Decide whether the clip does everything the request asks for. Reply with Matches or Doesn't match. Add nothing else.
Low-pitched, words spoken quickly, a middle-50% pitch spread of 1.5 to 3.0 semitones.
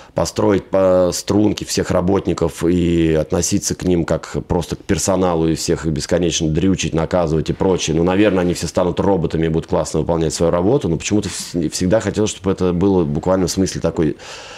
Matches